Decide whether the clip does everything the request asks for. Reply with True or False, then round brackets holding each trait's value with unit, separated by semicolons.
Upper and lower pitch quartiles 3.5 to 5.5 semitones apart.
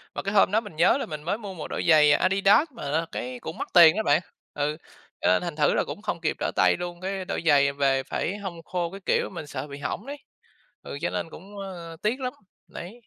True (4.8 semitones)